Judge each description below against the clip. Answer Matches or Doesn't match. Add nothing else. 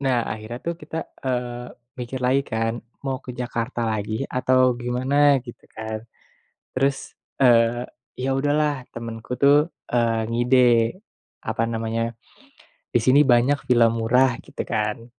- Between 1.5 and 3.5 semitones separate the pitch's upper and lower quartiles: Matches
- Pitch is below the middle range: Matches